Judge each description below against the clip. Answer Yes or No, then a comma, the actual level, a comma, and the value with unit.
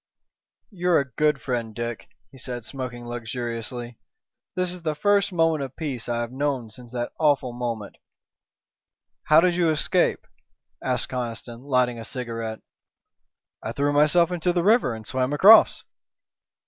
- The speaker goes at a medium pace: Yes, average, 150 wpm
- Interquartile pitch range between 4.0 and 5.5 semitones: Yes, average, 5.0 semitones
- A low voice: Yes, low, 130 Hz